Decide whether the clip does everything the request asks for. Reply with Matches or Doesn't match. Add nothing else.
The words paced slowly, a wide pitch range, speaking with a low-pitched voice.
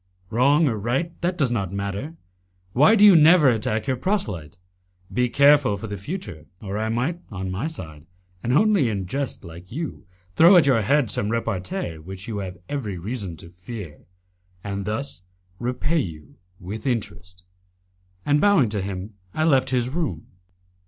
Doesn't match